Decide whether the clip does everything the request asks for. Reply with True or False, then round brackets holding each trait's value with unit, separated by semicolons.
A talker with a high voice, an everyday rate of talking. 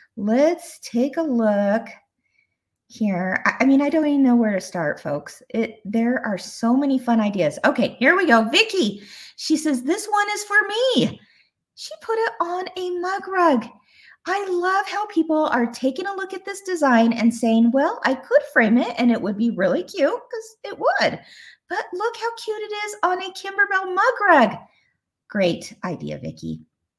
True (280 Hz; 180 wpm)